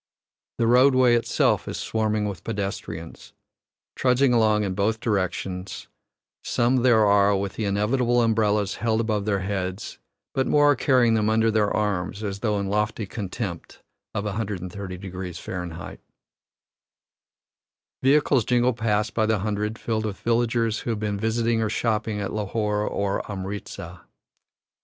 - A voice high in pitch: No, low, 105 Hz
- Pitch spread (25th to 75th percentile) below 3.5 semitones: Yes, narrow, 2.5 semitones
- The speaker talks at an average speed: Yes, average, 145 wpm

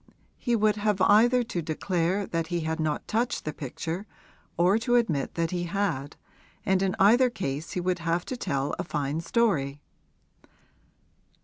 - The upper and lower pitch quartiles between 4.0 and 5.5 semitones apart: Yes, average, 4.8 semitones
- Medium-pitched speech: Yes, medium, 180 Hz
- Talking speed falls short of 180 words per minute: Yes, average, 165 wpm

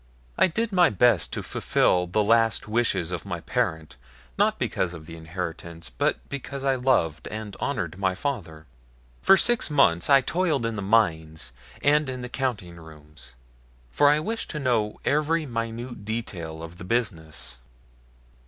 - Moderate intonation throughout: No, wide, 8.0 semitones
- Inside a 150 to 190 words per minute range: Yes, average, 160 wpm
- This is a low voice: Yes, low, 110 Hz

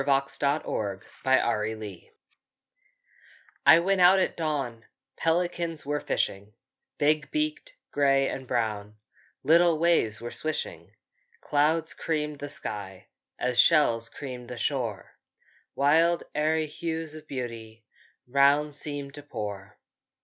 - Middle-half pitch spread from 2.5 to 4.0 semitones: No, average, 5.1 semitones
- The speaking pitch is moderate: Yes, medium, 145 Hz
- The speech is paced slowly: Yes, slow, 120 wpm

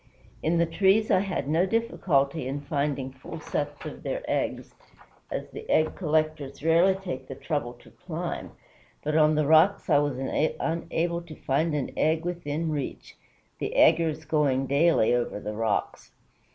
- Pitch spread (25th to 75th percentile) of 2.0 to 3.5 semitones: Yes, average, 3.2 semitones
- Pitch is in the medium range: Yes, medium, 155 Hz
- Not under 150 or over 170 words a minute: Yes, average, 160 wpm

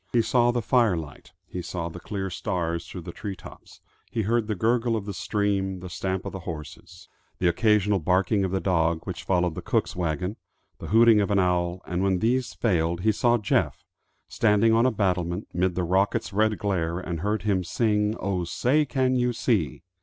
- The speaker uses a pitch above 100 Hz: No, very low, 95 Hz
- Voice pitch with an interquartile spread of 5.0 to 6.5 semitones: No, average, 3.8 semitones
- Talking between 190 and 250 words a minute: Yes, average, 200 wpm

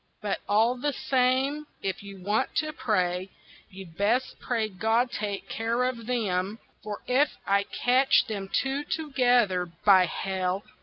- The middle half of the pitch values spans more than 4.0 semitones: Yes, average, 4.6 semitones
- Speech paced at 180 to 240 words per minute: No, average, 145 wpm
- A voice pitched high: Yes, high, 220 Hz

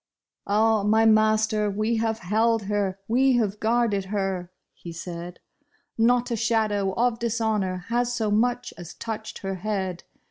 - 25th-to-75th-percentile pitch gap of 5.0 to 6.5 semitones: No, average, 2.8 semitones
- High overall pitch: Yes, high, 215 Hz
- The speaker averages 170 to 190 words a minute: No, average, 155 wpm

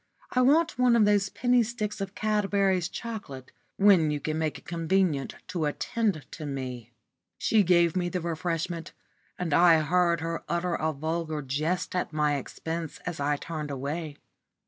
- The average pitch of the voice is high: No, medium, 170 Hz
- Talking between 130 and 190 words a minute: Yes, average, 165 wpm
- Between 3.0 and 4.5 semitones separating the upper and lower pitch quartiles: Yes, average, 4.2 semitones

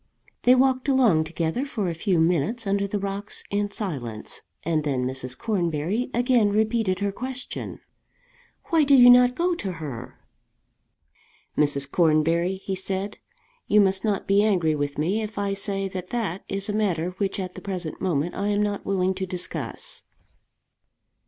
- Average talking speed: Yes, average, 165 wpm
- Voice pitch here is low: No, high, 195 Hz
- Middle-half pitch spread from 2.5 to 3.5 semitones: No, average, 4.2 semitones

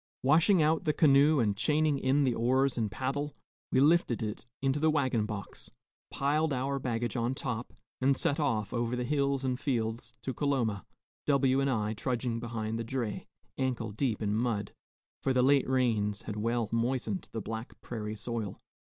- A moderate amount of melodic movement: Yes, average, 3.6 semitones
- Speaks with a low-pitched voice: Yes, low, 125 Hz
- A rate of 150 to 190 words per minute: Yes, average, 175 wpm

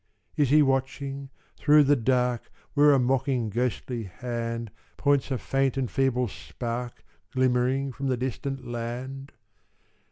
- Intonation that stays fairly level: Yes, narrow, 2.0 semitones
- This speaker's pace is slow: Yes, slow, 130 wpm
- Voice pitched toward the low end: Yes, low, 130 Hz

